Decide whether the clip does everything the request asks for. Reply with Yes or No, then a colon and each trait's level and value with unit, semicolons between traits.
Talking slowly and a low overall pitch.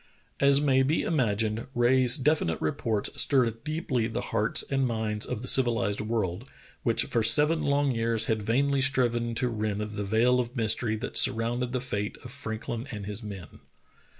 No: average, 180 wpm; low, 115 Hz